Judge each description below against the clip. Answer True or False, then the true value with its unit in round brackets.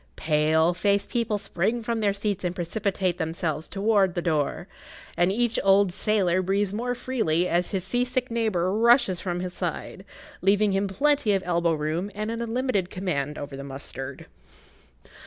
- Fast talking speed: False (165 wpm)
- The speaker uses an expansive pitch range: False (4.1 semitones)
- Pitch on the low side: False (195 Hz)